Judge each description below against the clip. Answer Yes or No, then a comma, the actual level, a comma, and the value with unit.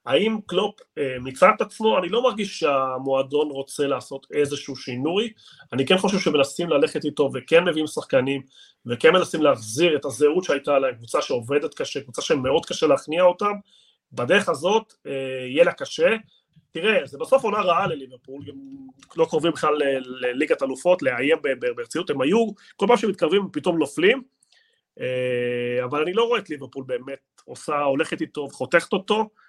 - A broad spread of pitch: Yes, wide, 8.3 semitones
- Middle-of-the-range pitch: Yes, medium, 165 Hz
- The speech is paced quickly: Yes, fast, 155 wpm